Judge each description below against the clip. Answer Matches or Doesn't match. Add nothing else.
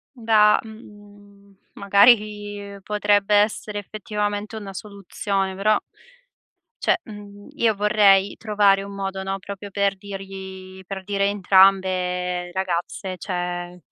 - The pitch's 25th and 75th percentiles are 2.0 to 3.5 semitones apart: Doesn't match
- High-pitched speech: Matches